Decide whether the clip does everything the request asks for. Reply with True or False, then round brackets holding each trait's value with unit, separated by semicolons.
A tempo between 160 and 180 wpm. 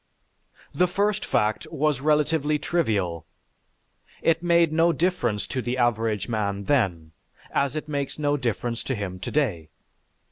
False (135 wpm)